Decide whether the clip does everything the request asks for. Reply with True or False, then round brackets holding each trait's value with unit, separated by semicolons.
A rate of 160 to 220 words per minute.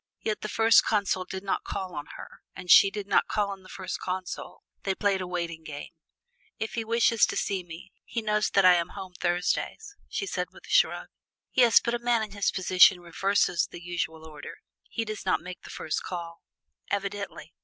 True (205 wpm)